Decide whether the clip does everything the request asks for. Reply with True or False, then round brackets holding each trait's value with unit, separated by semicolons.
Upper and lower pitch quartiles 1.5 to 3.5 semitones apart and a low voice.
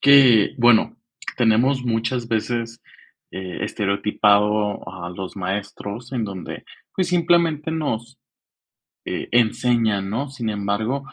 False (4.0 semitones; 115 Hz)